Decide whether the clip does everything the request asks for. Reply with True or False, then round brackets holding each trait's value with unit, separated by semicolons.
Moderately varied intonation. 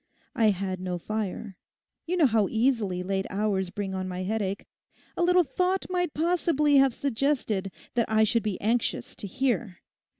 False (6.2 semitones)